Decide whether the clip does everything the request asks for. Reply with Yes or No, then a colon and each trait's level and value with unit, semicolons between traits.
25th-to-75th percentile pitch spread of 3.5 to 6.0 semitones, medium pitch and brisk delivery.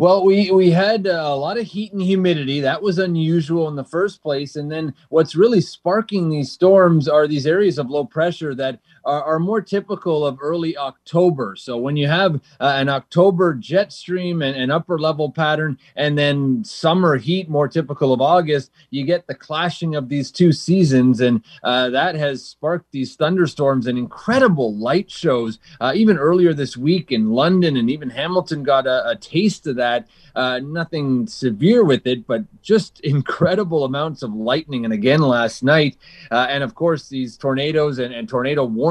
No: average, 4.6 semitones; medium, 155 Hz; average, 185 wpm